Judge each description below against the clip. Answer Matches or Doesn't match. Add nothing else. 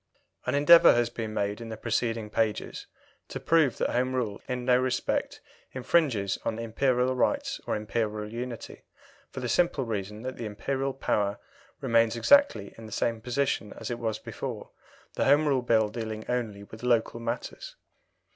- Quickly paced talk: Doesn't match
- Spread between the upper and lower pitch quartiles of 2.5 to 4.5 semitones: Matches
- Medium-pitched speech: Doesn't match